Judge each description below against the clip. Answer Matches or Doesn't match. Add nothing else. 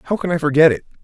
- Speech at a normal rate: Doesn't match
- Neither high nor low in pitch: Matches